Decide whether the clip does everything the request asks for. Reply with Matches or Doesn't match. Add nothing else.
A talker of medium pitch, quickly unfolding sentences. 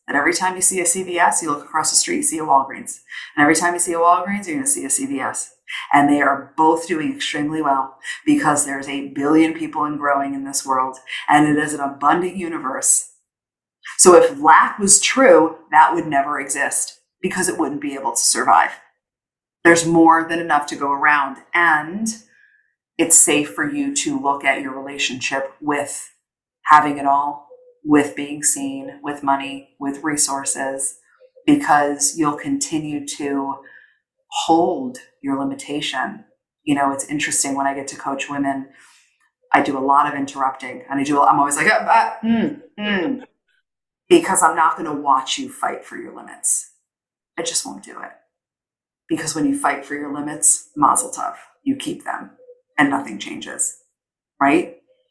Doesn't match